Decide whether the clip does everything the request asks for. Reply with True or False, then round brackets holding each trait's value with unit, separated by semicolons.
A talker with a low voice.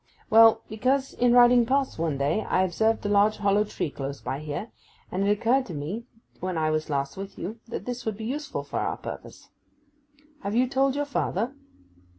False (215 Hz)